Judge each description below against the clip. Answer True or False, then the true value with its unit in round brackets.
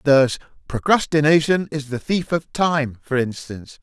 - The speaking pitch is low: False (145 Hz)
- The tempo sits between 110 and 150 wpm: True (140 wpm)